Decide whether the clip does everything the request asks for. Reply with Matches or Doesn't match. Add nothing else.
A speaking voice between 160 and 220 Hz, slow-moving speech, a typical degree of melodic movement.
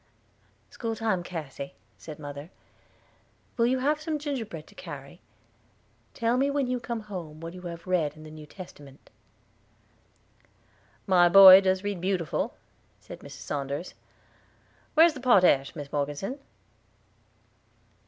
Doesn't match